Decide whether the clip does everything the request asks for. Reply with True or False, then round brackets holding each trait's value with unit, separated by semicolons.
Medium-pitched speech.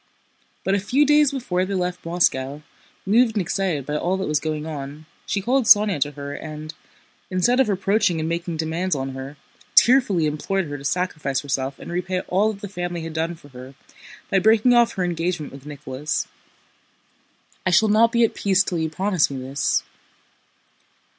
True (175 Hz)